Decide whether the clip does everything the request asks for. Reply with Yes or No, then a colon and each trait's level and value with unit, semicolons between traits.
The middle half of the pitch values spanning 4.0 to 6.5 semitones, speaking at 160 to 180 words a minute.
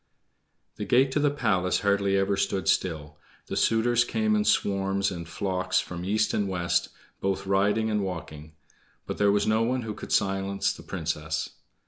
No: average, 2.9 semitones; average, 170 wpm